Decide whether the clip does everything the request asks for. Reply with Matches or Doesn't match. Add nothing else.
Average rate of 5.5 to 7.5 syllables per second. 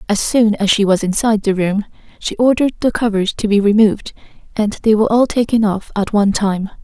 Matches